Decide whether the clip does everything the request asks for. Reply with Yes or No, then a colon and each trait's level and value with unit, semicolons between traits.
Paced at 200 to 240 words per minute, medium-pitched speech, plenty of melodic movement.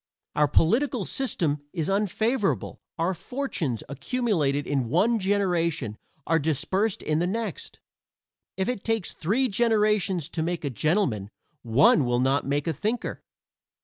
No: slow, 135 wpm; medium, 175 Hz; wide, 6.9 semitones